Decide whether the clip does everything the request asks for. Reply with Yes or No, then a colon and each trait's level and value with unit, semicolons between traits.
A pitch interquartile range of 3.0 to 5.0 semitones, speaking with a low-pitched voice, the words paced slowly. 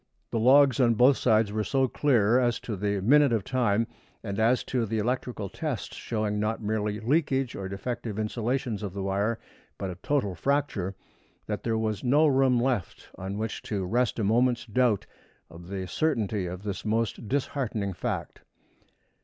No: average, 3.8 semitones; low, 110 Hz; average, 170 wpm